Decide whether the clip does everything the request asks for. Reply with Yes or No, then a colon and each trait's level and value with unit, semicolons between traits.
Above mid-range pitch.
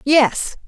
Yes: very high, 260 Hz